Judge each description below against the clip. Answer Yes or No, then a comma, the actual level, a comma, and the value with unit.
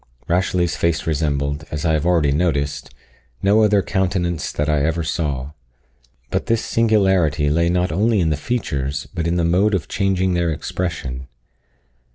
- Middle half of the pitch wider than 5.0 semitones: No, average, 4.1 semitones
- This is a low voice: Yes, very low, 85 Hz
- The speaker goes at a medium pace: Yes, average, 160 wpm